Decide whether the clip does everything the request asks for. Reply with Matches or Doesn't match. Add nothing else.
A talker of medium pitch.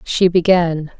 Matches